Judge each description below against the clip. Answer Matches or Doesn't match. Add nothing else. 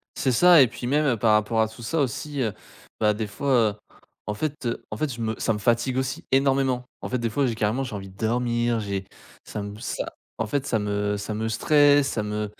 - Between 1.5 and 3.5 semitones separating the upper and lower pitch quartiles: Doesn't match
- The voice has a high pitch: Doesn't match